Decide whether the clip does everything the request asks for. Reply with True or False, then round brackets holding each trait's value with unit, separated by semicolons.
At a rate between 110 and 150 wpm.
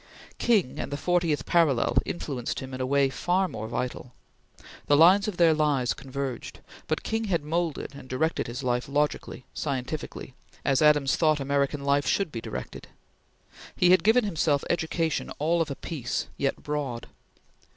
False (160 wpm)